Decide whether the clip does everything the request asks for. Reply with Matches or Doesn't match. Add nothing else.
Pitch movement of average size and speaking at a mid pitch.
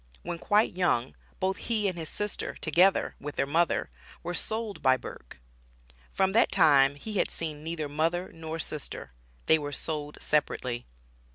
Matches